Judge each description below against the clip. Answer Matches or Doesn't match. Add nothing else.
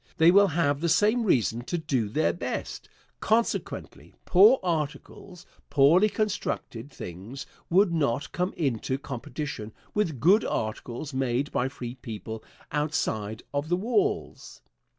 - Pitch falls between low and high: Matches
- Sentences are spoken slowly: Matches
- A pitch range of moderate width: Doesn't match